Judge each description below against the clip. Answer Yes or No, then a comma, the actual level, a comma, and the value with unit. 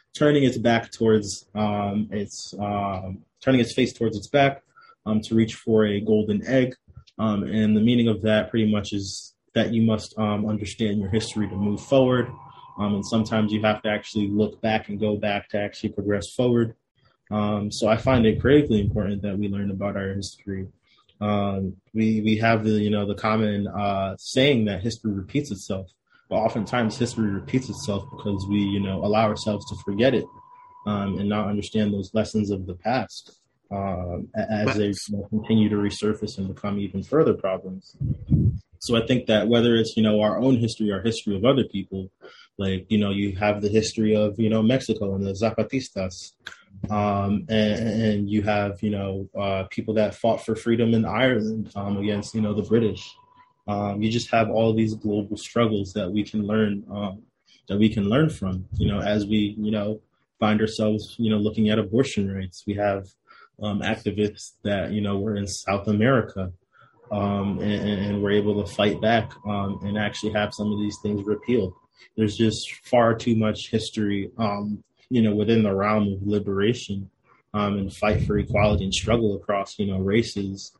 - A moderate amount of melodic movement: No, narrow, 1.6 semitones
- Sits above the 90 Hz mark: Yes, low, 105 Hz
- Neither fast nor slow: Yes, average, 190 wpm